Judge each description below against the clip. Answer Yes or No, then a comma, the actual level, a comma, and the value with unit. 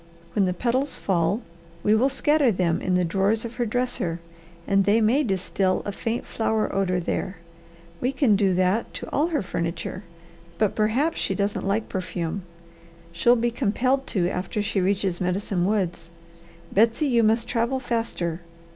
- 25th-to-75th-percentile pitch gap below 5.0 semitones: Yes, average, 4.2 semitones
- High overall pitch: Yes, high, 205 Hz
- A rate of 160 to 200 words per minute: Yes, average, 165 wpm